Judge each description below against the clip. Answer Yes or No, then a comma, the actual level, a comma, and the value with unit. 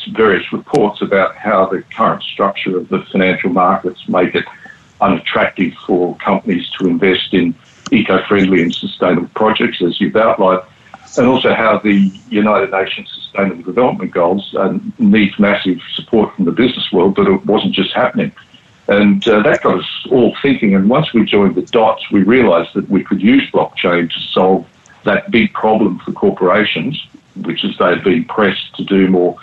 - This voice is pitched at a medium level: No, very low, 95 Hz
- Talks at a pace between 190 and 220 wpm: No, average, 170 wpm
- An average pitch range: No, narrow, 2.1 semitones